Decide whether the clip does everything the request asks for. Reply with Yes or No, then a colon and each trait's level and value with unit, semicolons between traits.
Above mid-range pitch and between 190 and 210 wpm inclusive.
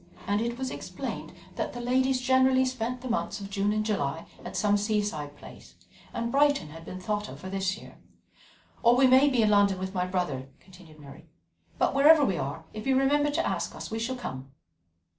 Yes: high, 215 Hz; fast, 205 wpm